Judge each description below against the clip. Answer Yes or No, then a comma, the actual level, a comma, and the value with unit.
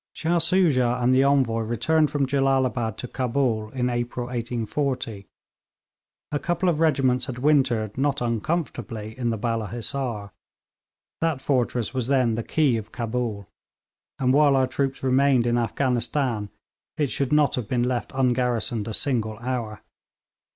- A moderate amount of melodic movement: Yes, average, 3.1 semitones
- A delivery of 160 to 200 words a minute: No, average, 145 wpm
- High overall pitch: No, low, 125 Hz